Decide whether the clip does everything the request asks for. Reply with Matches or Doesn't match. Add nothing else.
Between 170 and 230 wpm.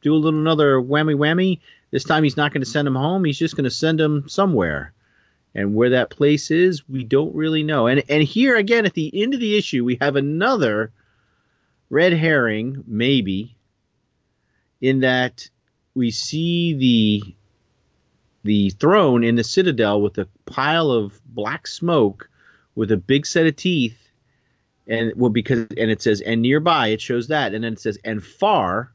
Matches